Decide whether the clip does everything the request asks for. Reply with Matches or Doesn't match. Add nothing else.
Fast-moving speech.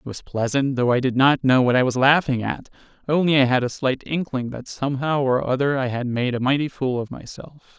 Matches